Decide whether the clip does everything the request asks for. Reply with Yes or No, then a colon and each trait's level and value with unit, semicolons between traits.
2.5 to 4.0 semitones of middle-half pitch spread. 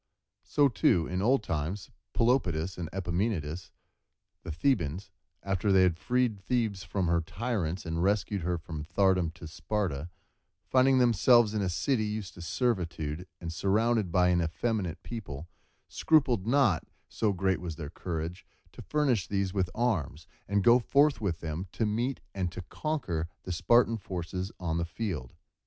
No: average, 5.2 semitones